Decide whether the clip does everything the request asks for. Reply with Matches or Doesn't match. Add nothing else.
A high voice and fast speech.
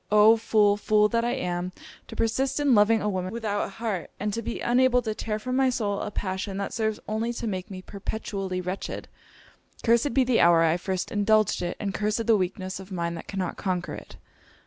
Matches